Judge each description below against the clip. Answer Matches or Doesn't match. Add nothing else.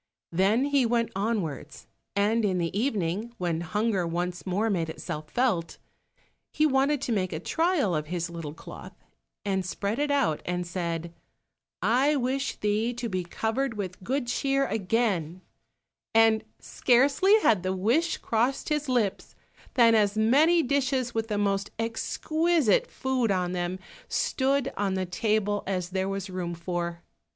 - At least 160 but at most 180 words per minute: Doesn't match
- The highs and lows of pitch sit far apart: Matches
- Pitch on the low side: Doesn't match